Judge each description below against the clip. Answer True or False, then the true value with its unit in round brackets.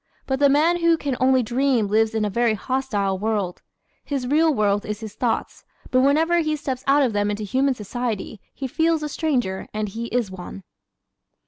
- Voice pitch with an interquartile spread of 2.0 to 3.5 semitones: False (4.9 semitones)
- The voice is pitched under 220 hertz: False (245 Hz)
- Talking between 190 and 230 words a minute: True (195 wpm)